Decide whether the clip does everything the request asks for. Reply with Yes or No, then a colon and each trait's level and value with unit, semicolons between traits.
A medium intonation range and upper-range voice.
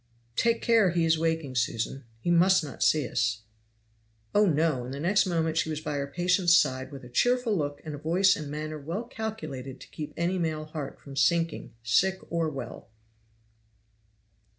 No: average, 4.3 semitones; medium, 160 Hz